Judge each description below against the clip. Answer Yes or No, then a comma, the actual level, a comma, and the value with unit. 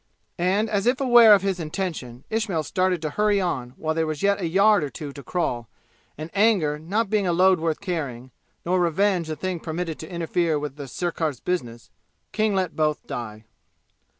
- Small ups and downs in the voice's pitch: No, average, 4.4 semitones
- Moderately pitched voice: Yes, medium, 170 Hz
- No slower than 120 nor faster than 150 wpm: No, average, 190 wpm